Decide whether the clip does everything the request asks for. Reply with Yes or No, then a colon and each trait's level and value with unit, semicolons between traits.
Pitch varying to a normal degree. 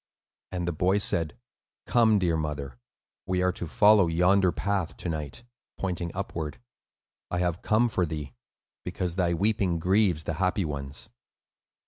Yes: average, 3.3 semitones